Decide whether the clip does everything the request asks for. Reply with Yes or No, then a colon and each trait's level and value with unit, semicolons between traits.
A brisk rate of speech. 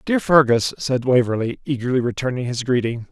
No: average, 155 wpm